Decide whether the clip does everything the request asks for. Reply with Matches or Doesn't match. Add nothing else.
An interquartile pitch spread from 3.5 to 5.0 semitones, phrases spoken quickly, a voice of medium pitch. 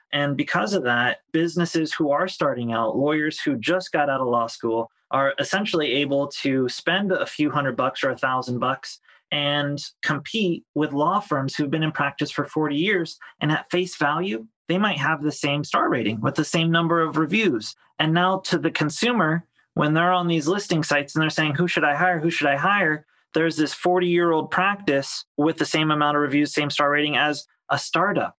Doesn't match